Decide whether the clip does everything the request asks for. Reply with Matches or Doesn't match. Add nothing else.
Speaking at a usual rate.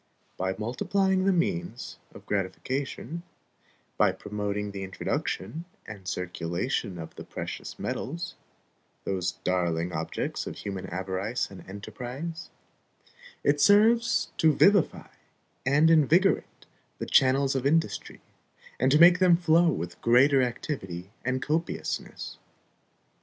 Doesn't match